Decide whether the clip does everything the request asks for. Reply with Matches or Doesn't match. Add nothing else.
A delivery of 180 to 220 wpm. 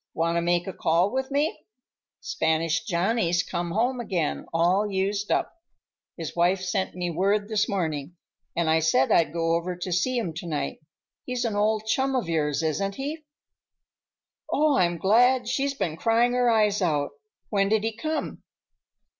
Doesn't match